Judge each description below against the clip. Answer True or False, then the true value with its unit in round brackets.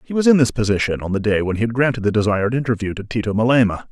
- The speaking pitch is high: False (115 Hz)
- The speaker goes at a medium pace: False (275 wpm)